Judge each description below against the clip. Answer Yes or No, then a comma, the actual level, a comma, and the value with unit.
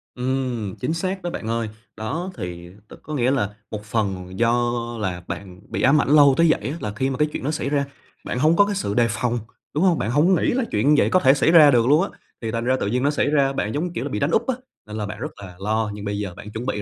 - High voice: No, low, 125 Hz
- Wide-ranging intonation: Yes, wide, 6.1 semitones